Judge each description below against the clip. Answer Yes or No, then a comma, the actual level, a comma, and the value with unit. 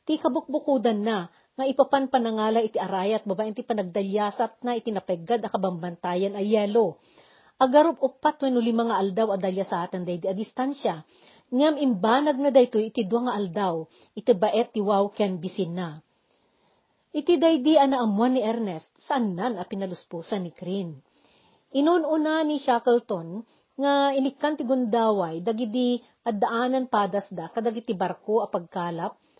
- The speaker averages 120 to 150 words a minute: Yes, average, 145 wpm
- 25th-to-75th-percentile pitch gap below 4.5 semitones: No, average, 5.1 semitones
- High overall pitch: Yes, high, 225 Hz